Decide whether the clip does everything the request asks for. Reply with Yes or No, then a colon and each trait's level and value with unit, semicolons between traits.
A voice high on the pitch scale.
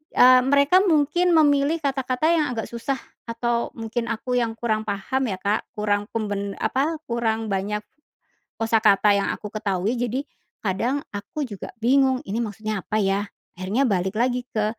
Yes: high, 230 Hz